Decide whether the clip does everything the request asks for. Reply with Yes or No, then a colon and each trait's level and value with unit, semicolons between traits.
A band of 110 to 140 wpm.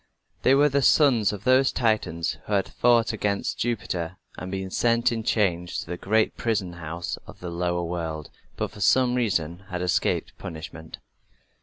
No: average, 170 wpm